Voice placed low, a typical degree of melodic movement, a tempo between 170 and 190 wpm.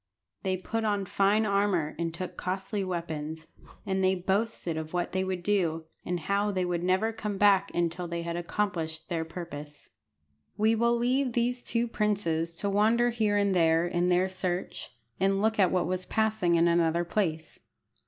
No: medium, 185 Hz; average, 3.4 semitones; average, 175 wpm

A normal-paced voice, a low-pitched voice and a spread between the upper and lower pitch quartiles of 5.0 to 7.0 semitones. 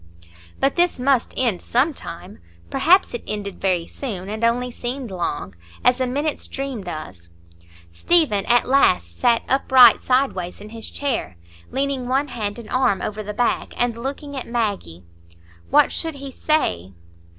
No: average, 155 wpm; high, 240 Hz; average, 5.3 semitones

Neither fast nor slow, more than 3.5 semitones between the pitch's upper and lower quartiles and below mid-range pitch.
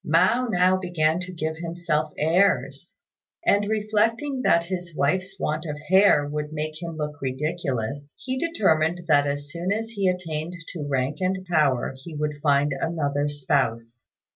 No: average, 155 wpm; average, 4.1 semitones; medium, 160 Hz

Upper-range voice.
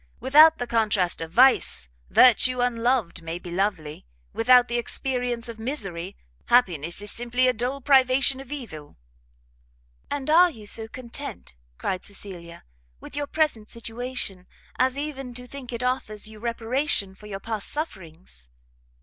Yes: high, 235 Hz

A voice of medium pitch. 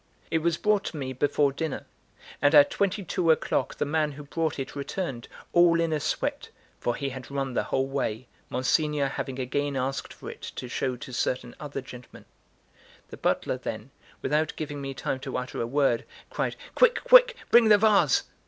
Yes: medium, 145 Hz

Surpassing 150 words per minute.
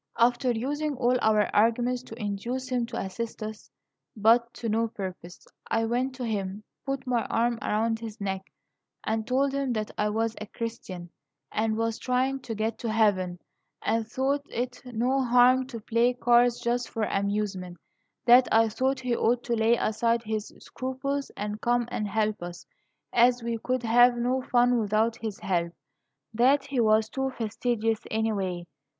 Yes: average, 170 wpm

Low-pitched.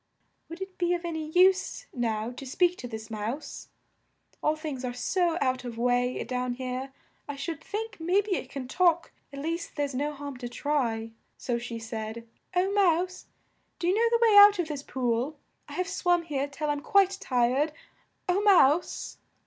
No: very high, 290 Hz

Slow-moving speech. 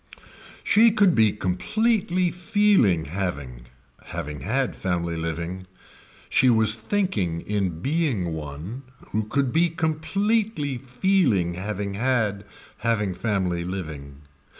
Yes: slow, 105 wpm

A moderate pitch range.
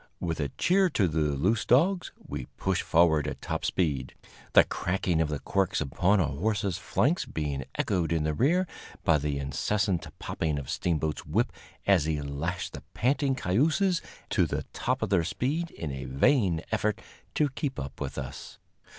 No: wide, 7.0 semitones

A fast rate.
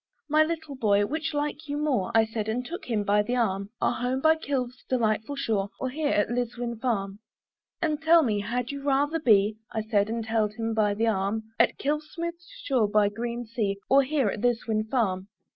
Yes: fast, 210 wpm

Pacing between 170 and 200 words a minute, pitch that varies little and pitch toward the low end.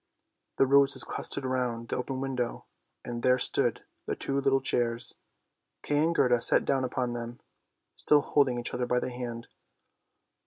No: average, 160 wpm; narrow, 2.0 semitones; low, 125 Hz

